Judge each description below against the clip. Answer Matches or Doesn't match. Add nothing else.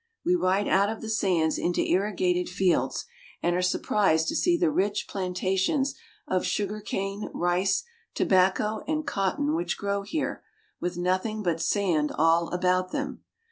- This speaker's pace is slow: Doesn't match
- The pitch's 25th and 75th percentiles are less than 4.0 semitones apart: Matches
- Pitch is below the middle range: Doesn't match